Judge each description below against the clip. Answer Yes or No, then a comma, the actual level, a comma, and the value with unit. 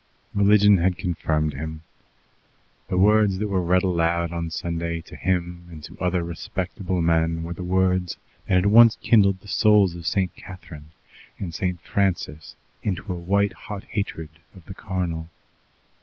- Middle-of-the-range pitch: No, very low, 90 Hz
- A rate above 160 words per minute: No, average, 155 wpm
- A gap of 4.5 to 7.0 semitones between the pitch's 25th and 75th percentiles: No, average, 2.7 semitones